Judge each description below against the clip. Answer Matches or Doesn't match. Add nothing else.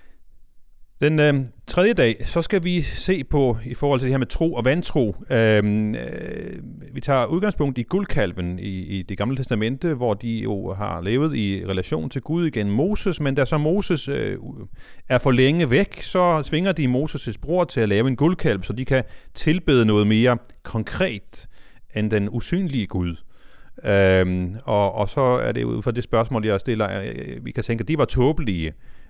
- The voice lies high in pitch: Doesn't match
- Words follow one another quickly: Doesn't match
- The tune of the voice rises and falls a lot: Matches